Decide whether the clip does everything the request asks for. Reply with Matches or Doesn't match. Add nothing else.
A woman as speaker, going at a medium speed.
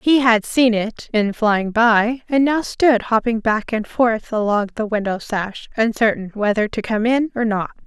Matches